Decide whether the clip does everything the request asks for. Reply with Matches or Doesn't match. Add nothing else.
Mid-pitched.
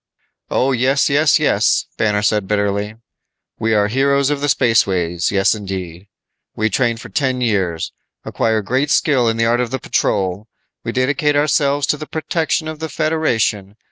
Doesn't match